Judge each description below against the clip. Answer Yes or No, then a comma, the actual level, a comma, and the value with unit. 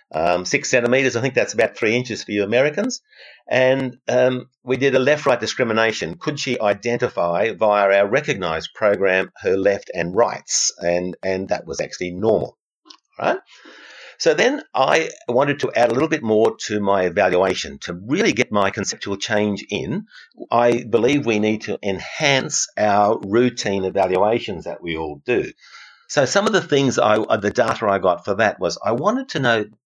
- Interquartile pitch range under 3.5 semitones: No, average, 4.2 semitones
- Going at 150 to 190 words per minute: Yes, average, 180 wpm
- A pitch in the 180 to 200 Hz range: No, low, 110 Hz